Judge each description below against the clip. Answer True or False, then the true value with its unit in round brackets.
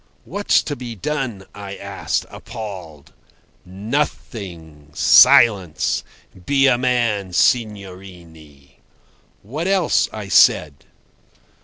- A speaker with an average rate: False (90 wpm)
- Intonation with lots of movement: True (5.8 semitones)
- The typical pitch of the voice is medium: False (100 Hz)